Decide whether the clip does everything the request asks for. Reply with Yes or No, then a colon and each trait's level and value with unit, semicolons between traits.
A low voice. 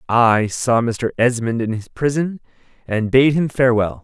Yes: low, 120 Hz